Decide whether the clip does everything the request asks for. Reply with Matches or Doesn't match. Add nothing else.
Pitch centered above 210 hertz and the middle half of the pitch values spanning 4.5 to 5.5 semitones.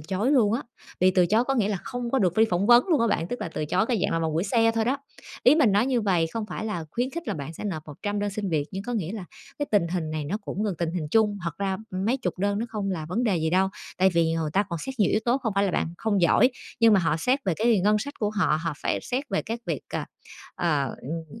Doesn't match